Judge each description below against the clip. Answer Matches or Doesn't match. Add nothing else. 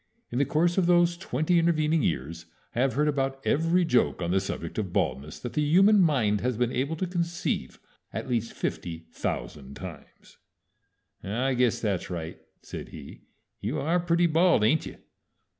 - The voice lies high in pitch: Doesn't match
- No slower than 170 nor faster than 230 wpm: Matches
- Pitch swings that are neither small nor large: Doesn't match